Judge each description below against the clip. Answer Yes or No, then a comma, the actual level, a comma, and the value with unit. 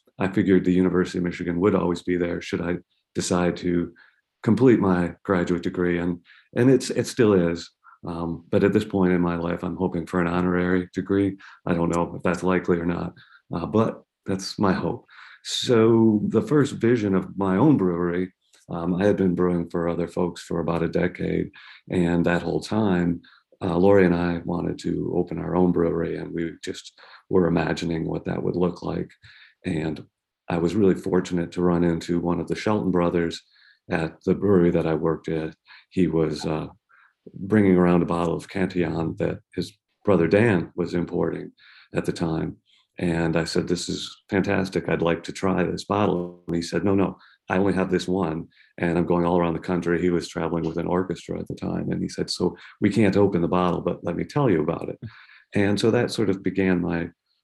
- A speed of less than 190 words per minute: No, fast, 205 wpm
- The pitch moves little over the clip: Yes, narrow, 1.7 semitones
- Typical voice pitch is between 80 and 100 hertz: Yes, very low, 90 Hz